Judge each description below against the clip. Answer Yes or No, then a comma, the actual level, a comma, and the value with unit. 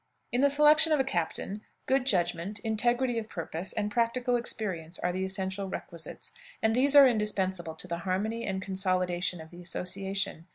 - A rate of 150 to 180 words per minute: Yes, average, 170 wpm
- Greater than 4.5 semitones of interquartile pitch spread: Yes, average, 5.0 semitones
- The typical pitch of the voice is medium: No, high, 195 Hz